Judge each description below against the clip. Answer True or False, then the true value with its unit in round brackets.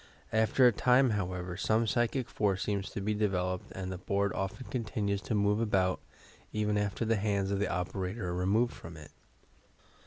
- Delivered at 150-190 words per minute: True (185 wpm)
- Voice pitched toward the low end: True (100 Hz)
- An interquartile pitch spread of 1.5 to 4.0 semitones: True (2.9 semitones)